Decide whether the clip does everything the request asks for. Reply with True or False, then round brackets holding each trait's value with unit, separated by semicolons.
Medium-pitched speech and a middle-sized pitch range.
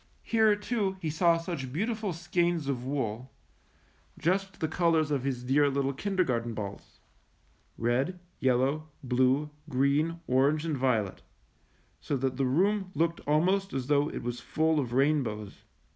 True (145 Hz; 4.8 semitones)